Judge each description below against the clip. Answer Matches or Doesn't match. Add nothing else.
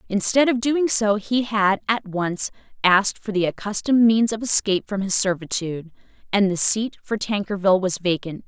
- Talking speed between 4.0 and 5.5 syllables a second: Matches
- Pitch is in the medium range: Doesn't match